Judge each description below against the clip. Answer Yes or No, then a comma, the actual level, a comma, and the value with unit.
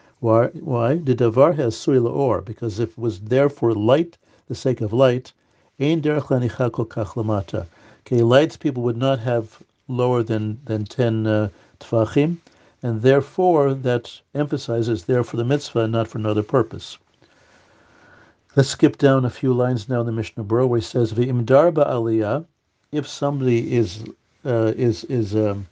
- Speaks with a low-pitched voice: Yes, low, 120 Hz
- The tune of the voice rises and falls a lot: No, average, 3.4 semitones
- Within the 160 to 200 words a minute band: No, average, 145 wpm